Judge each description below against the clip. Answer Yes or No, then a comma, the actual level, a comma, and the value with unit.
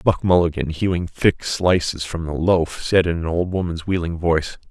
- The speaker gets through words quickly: No, average, 190 wpm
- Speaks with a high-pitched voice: No, very low, 85 Hz